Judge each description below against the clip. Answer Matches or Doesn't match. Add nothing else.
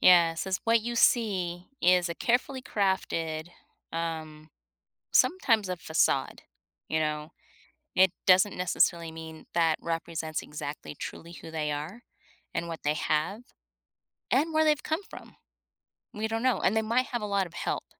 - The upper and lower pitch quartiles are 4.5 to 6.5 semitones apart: Matches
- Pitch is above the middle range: Doesn't match